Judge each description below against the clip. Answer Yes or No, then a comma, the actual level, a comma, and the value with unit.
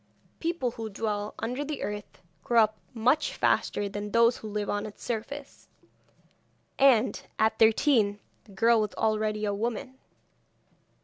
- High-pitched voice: Yes, high, 220 Hz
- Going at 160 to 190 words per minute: No, average, 140 wpm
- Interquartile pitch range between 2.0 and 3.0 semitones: Yes, narrow, 2.4 semitones